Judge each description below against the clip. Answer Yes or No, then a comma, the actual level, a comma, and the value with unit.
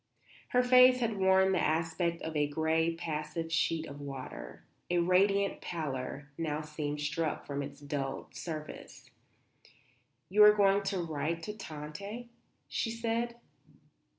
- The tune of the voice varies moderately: Yes, average, 4.8 semitones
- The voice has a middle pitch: Yes, medium, 165 Hz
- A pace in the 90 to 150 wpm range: Yes, slow, 135 wpm